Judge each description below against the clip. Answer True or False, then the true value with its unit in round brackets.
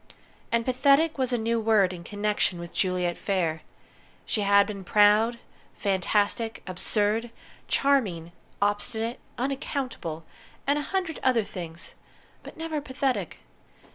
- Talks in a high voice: True (215 Hz)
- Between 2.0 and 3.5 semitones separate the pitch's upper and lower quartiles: False (5.3 semitones)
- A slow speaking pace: True (120 wpm)